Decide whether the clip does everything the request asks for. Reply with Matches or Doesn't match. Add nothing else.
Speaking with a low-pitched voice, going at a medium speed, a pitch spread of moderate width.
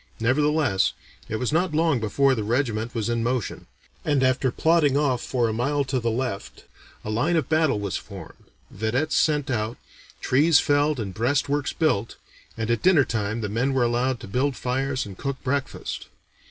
Matches